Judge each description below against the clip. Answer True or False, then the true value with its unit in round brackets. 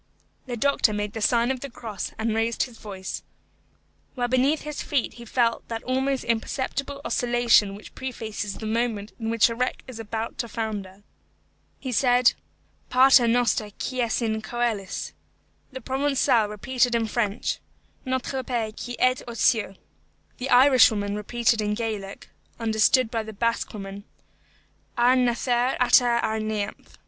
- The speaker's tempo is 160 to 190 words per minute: False (150 wpm)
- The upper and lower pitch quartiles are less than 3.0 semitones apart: True (2.6 semitones)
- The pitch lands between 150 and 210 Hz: False (235 Hz)